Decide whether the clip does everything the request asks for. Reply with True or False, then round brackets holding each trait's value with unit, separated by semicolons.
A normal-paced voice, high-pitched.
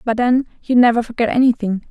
True (190 wpm; 235 Hz)